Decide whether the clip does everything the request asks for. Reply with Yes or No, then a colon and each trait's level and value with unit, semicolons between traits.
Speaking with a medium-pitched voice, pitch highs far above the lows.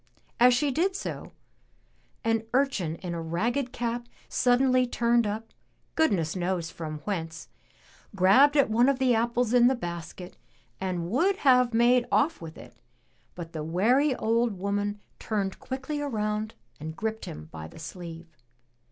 No: high, 220 Hz; wide, 6.2 semitones